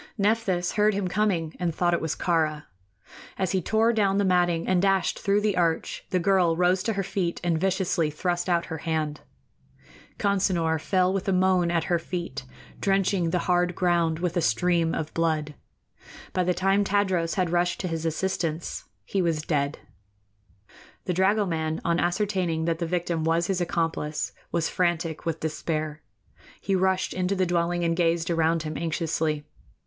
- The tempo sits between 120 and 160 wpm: No, average, 170 wpm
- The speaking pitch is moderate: Yes, medium, 175 Hz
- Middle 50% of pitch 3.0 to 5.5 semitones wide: No, narrow, 2.5 semitones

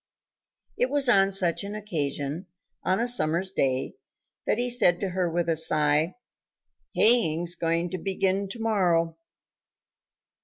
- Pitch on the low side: No, medium, 185 Hz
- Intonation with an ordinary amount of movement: Yes, average, 3.7 semitones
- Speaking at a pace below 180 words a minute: Yes, average, 140 wpm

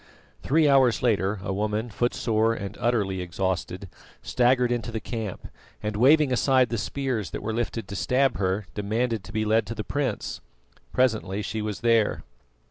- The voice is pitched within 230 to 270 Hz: No, low, 110 Hz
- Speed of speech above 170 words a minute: No, average, 165 wpm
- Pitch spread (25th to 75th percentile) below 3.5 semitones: Yes, average, 3.0 semitones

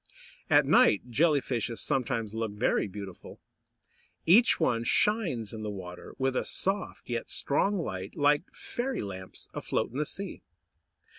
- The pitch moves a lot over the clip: Yes, wide, 7.5 semitones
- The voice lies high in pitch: No, low, 120 Hz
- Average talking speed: Yes, average, 145 wpm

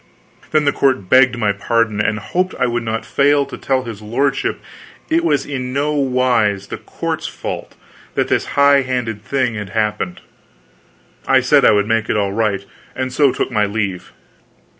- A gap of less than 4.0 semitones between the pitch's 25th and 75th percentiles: No, average, 4.5 semitones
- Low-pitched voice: Yes, low, 120 Hz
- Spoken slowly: No, average, 180 wpm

